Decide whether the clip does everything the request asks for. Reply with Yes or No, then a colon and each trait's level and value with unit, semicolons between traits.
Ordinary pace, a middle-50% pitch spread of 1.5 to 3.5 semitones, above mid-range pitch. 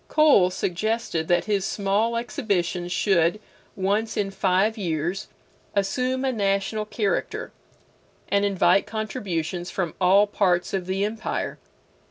No: slow, 120 wpm; average, 3.1 semitones; high, 195 Hz